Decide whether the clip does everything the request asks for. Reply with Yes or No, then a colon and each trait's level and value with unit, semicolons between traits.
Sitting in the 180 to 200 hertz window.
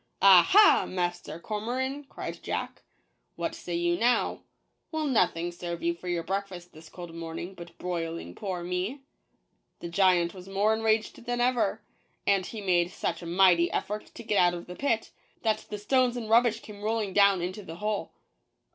Yes: high, 190 Hz